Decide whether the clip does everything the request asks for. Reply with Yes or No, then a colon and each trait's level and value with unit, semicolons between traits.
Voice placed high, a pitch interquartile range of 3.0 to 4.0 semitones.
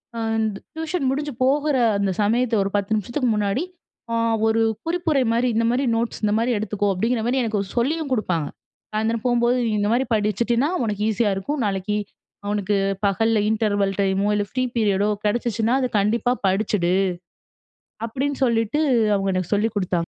Yes: high, 225 Hz; average, 3.3 semitones